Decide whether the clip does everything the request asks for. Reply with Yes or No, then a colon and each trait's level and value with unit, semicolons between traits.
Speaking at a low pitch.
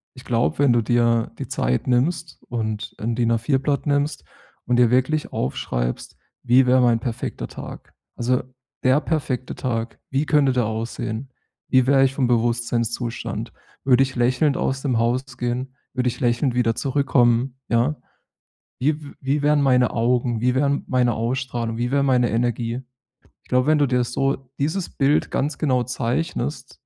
Yes: low, 125 Hz